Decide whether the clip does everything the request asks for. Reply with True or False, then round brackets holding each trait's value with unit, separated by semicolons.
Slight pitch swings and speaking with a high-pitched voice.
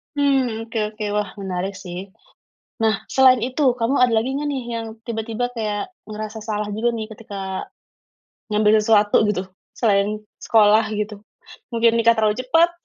True (2.3 semitones; 220 Hz)